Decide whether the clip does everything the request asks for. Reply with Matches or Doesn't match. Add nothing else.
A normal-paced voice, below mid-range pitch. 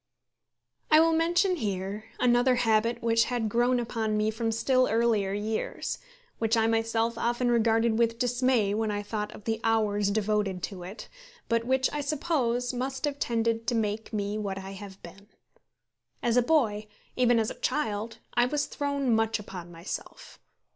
Doesn't match